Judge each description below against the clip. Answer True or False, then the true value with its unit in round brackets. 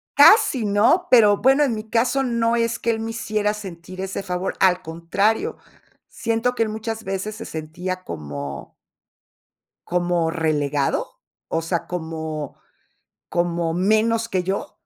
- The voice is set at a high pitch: True (195 Hz)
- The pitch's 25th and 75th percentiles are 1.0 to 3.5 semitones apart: False (5.1 semitones)